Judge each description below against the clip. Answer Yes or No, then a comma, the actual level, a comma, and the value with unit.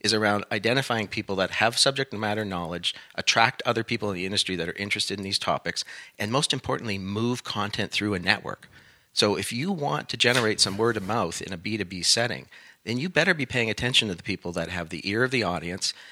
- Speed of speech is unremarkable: No, fast, 220 wpm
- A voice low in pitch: Yes, low, 105 Hz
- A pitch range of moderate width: Yes, average, 3.5 semitones